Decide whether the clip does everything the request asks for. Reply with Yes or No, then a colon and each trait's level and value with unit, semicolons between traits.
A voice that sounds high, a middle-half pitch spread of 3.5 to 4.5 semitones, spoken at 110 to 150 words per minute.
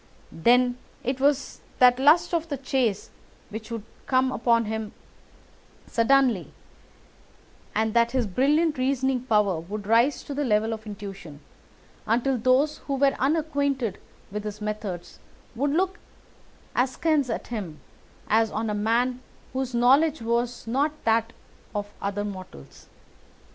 Yes: high, 240 Hz; average, 4.1 semitones; slow, 135 wpm